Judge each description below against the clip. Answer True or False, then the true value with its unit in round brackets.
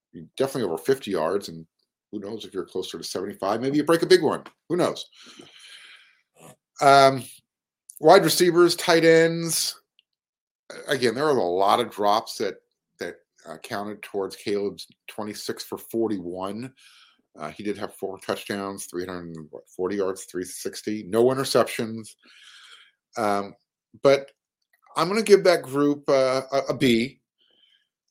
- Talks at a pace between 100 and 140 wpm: True (135 wpm)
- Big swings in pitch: True (6.9 semitones)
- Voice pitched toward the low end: True (120 Hz)